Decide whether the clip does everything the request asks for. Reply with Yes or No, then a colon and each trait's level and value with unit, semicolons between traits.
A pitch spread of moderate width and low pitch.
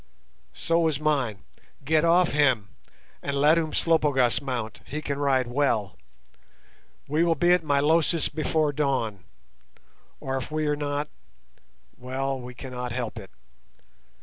No: average, 3.5 semitones; medium, 145 Hz